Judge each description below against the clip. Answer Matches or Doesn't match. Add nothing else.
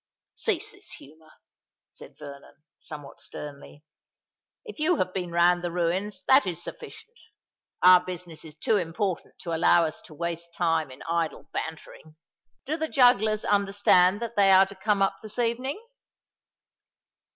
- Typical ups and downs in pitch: Matches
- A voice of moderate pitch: Matches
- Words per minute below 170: Matches